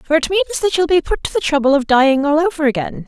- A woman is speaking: Yes, female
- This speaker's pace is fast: Yes, fast, 290 wpm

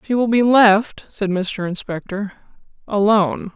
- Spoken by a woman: Yes, female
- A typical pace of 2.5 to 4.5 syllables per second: Yes, 4.1 syllables/s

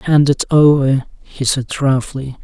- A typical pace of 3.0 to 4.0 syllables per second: Yes, 3.9 syllables/s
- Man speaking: Yes, male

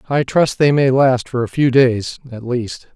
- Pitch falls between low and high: No, low, 130 Hz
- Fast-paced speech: Yes, fast, 225 wpm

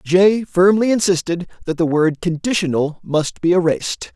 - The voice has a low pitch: No, medium, 175 Hz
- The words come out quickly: No, average, 145 wpm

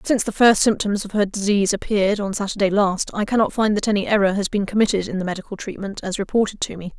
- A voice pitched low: No, high, 200 Hz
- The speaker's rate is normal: No, fast, 240 wpm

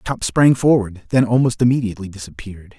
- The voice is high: No, low, 110 Hz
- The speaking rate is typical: Yes, average, 150 wpm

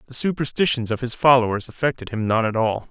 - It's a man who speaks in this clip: Yes, male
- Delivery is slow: No, fast, 205 wpm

